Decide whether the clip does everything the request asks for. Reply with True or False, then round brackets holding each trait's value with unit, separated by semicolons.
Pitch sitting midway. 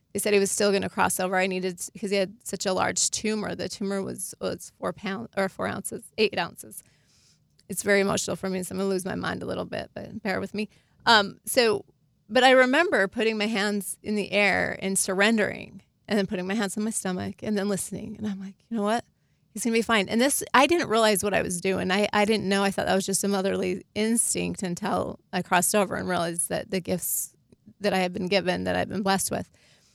False (195 Hz)